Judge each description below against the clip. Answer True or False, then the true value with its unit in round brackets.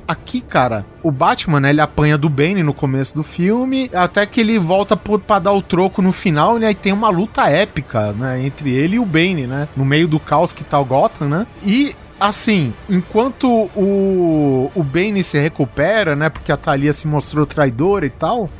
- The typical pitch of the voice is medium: True (165 Hz)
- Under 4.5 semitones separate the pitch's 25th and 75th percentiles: False (5.6 semitones)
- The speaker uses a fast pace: True (205 wpm)